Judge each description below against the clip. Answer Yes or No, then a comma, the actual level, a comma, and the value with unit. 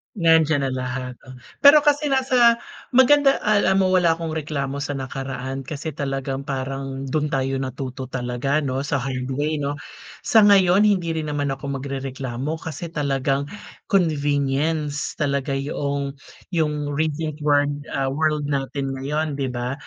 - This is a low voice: No, medium, 145 Hz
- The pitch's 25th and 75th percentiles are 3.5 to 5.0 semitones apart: No, average, 2.9 semitones